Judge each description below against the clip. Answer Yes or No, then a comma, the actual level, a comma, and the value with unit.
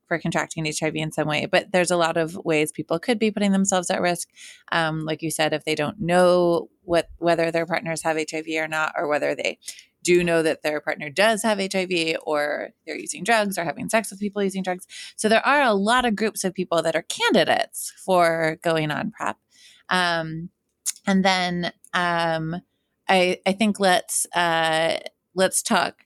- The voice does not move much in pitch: No, average, 3.0 semitones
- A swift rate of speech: No, average, 195 wpm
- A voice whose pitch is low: No, medium, 170 Hz